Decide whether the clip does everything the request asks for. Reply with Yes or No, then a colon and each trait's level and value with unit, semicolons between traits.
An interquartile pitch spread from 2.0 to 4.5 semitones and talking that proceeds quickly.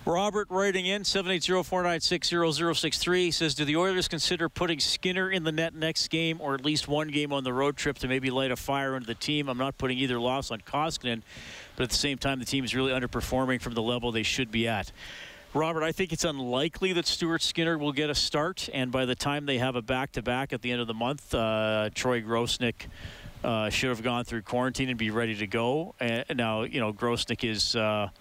No: average, 5.2 semitones; fast, 220 wpm